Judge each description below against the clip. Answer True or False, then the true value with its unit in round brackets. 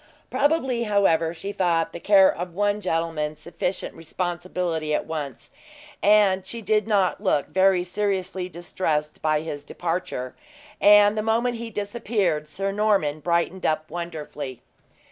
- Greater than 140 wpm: False (135 wpm)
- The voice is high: False (180 Hz)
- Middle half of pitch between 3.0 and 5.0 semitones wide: True (4.2 semitones)